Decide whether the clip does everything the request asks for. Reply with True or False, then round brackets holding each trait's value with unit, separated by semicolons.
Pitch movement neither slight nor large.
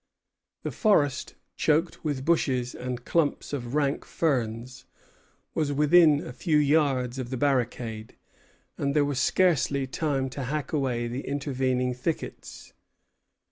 True (3.0 semitones)